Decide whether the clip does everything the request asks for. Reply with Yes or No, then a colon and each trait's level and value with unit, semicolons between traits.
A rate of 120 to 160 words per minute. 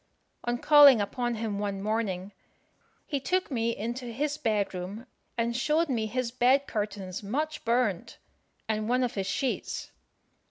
Yes: average, 150 wpm